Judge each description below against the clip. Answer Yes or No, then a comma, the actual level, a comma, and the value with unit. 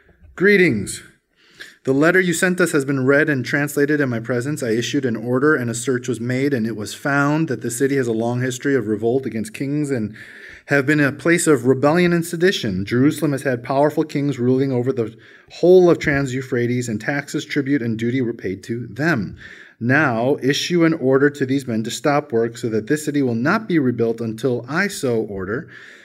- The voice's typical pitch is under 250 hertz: Yes, low, 135 Hz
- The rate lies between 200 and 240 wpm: Yes, fast, 205 wpm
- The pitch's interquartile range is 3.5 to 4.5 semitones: Yes, average, 4.0 semitones